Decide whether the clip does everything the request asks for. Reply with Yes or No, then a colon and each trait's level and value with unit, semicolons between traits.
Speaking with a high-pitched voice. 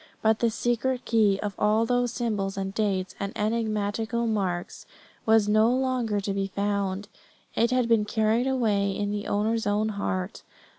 Yes: high, 215 Hz